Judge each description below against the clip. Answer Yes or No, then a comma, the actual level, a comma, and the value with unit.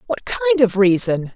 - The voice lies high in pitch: Yes, high, 230 Hz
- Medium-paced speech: Yes, average, 175 wpm